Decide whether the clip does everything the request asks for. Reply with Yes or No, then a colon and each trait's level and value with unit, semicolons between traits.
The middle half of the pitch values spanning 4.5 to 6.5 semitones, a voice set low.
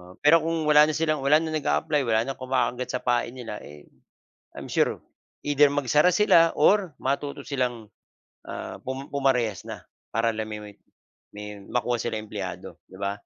Yes: average, 5.2 semitones; low, 130 Hz